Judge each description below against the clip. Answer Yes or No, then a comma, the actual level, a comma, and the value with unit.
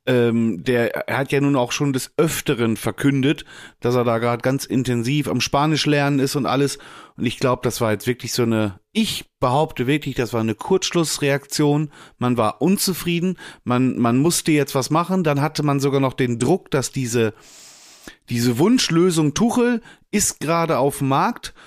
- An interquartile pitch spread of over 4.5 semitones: No, average, 3.8 semitones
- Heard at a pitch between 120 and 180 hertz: Yes, medium, 140 Hz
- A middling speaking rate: Yes, average, 180 wpm